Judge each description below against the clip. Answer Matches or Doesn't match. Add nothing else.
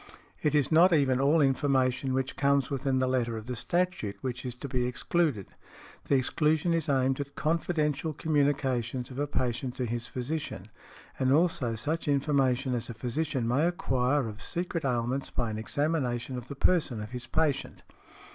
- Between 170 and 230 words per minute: Matches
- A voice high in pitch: Doesn't match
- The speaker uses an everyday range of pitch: Matches